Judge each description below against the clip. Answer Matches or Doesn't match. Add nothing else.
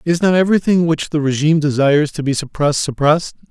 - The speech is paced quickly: Doesn't match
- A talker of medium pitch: Matches